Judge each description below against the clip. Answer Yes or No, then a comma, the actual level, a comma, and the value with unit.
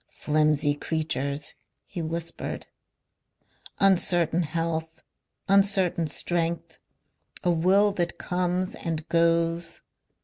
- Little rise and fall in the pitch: Yes, narrow, 1.9 semitones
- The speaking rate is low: Yes, slow, 80 wpm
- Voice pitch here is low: No, medium, 165 Hz